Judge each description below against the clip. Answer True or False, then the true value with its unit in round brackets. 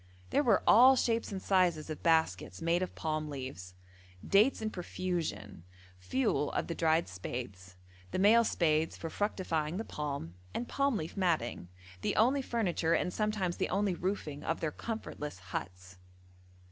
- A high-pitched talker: False (165 Hz)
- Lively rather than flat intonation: True (6.2 semitones)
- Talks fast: False (155 wpm)